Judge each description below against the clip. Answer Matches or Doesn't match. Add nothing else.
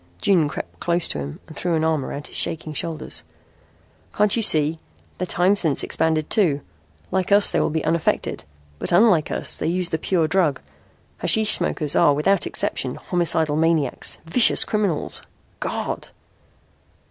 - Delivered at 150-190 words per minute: Matches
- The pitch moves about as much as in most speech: Matches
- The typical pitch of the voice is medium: Matches